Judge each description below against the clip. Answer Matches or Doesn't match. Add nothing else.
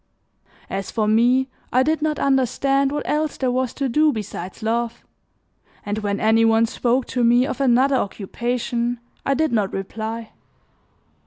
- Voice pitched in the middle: Doesn't match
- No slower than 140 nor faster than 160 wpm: Matches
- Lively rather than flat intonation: Doesn't match